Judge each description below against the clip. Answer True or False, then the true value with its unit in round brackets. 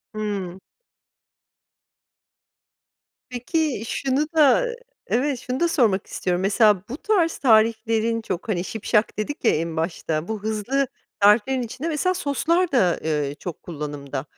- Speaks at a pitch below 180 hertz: False (220 Hz)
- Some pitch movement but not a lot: False (6.7 semitones)